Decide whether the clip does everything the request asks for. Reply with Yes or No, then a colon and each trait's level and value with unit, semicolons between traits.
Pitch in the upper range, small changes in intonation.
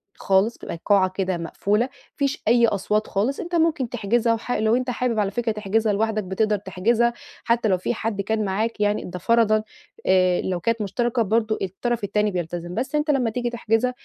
No: high, 220 Hz; average, 3.3 semitones